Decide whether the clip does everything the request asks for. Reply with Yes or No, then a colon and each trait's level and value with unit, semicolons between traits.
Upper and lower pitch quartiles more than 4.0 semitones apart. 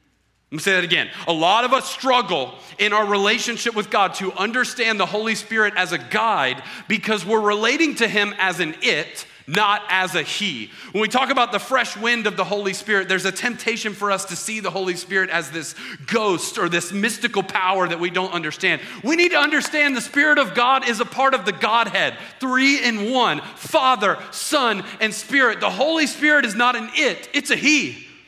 Yes: average, 4.6 semitones